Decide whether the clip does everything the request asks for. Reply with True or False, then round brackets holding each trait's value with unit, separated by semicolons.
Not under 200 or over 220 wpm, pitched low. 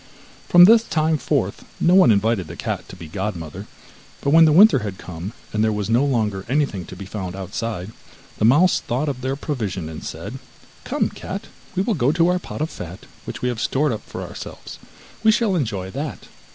True (205 wpm; 120 Hz)